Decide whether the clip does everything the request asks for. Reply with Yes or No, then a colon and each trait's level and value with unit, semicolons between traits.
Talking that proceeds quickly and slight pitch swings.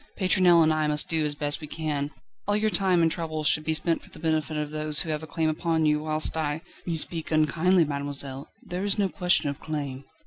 Yes: fast, 240 wpm; narrow, 1.9 semitones